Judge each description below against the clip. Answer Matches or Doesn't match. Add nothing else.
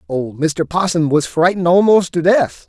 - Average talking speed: Matches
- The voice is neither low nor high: Matches